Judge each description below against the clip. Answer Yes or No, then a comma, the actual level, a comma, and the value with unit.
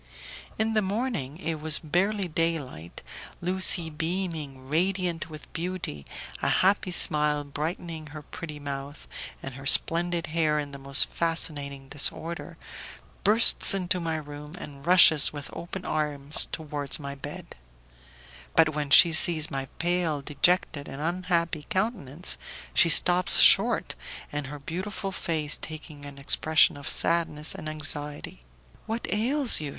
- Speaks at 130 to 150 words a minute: Yes, slow, 135 wpm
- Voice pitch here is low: No, medium, 155 Hz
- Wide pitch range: No, average, 3.4 semitones